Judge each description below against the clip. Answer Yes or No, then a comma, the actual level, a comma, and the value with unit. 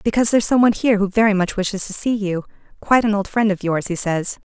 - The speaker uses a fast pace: Yes, fast, 265 wpm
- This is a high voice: Yes, high, 205 Hz